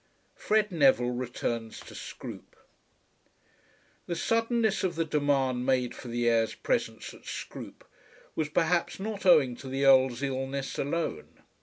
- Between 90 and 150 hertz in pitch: Yes, low, 135 Hz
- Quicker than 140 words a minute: No, slow, 135 wpm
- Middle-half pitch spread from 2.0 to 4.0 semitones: No, average, 5.2 semitones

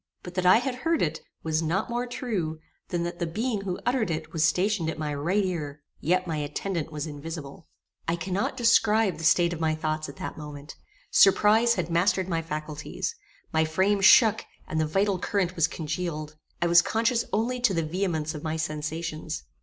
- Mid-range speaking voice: Yes, medium, 170 Hz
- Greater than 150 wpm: Yes, average, 195 wpm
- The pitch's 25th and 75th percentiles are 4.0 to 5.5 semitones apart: Yes, average, 4.3 semitones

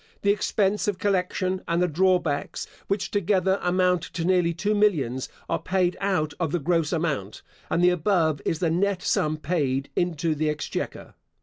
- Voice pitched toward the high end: No, medium, 175 Hz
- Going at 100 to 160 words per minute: No, average, 170 wpm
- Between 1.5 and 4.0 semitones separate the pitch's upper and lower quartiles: Yes, average, 3.3 semitones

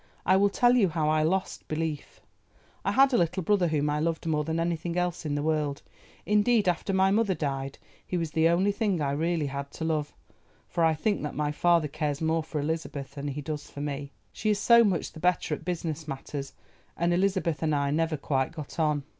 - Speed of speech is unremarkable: No, fast, 220 wpm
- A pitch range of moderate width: Yes, average, 3.2 semitones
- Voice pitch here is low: No, medium, 160 Hz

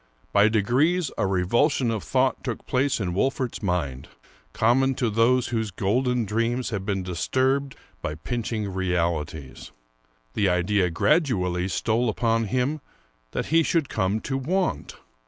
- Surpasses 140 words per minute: No, slow, 135 wpm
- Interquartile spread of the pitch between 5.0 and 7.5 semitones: Yes, wide, 5.5 semitones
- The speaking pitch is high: No, low, 110 Hz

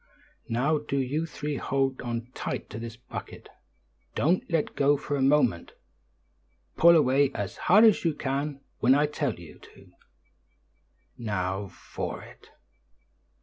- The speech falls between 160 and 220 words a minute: No, average, 140 wpm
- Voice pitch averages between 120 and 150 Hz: Yes, low, 135 Hz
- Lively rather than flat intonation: No, average, 4.3 semitones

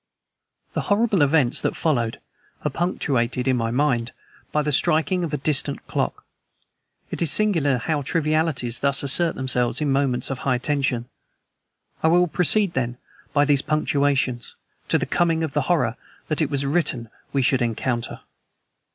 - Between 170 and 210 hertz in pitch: No, medium, 140 Hz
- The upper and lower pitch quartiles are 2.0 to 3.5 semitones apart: No, average, 4.0 semitones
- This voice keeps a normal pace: Yes, average, 160 wpm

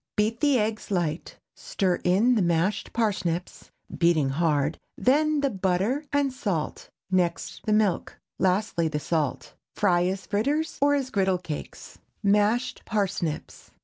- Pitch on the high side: Yes, high, 195 Hz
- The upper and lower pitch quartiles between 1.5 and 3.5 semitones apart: No, average, 5.2 semitones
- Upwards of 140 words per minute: No, slow, 135 wpm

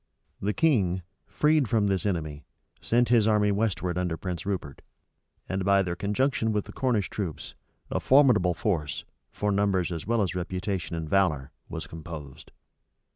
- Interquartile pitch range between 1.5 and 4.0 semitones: Yes, average, 3.5 semitones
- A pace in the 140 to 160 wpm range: Yes, average, 155 wpm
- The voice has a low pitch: Yes, very low, 95 Hz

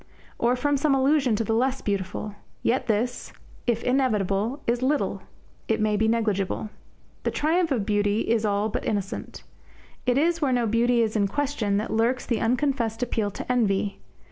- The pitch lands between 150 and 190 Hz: No, high, 230 Hz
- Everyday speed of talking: Yes, average, 170 wpm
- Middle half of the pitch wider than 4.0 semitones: No, average, 3.6 semitones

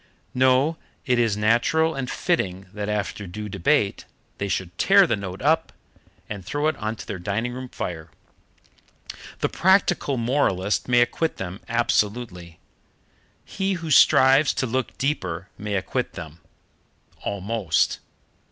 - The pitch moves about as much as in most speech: No, wide, 5.7 semitones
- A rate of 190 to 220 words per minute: No, slow, 135 wpm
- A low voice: Yes, low, 115 Hz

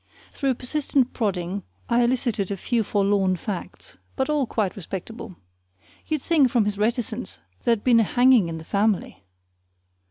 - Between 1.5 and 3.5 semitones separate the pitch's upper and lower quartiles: No, average, 4.1 semitones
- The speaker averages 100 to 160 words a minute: Yes, average, 150 wpm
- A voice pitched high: Yes, high, 220 Hz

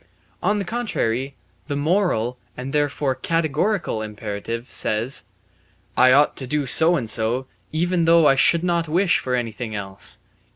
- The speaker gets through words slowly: No, average, 150 wpm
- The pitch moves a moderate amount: No, wide, 6.1 semitones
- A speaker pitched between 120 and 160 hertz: Yes, medium, 140 Hz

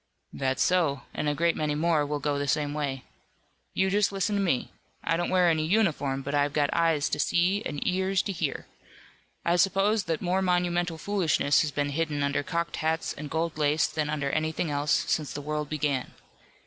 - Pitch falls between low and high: Yes, medium, 155 Hz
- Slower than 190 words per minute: No, average, 200 wpm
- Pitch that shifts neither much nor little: Yes, average, 3.4 semitones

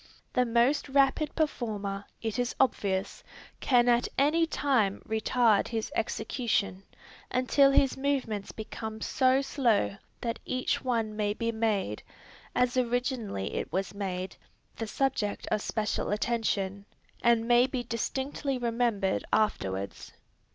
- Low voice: No, high, 230 Hz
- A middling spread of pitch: Yes, average, 3.7 semitones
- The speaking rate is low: Yes, slow, 125 wpm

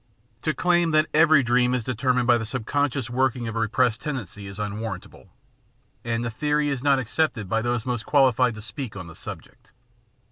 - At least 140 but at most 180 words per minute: No, average, 190 wpm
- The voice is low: Yes, low, 125 Hz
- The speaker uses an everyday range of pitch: Yes, average, 3.5 semitones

